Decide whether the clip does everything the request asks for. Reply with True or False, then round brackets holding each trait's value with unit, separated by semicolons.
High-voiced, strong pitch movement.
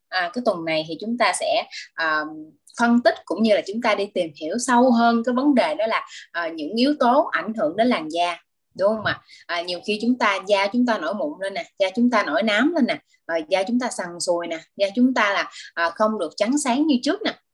True (235 Hz; 8.1 semitones)